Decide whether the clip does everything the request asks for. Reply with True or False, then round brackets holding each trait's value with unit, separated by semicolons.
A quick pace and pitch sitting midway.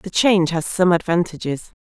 False (165 wpm; 175 Hz)